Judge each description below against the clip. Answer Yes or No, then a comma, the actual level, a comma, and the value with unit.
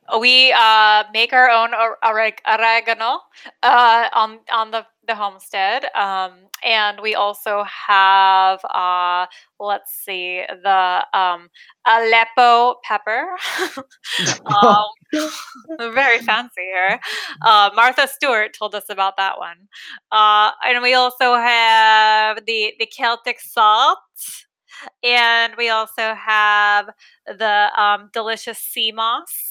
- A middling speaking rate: No, slow, 110 wpm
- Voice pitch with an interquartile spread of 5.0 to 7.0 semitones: No, average, 2.8 semitones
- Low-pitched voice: No, high, 225 Hz